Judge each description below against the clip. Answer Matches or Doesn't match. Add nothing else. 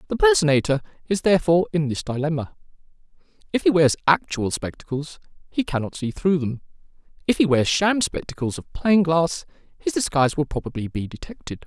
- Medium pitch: Matches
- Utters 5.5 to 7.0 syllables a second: Matches